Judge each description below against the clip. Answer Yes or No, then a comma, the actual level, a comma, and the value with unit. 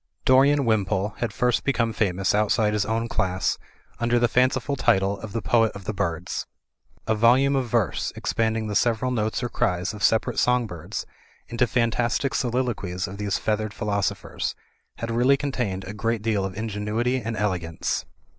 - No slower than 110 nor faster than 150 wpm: No, average, 170 wpm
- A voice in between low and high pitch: No, low, 110 Hz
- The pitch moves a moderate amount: Yes, average, 3.2 semitones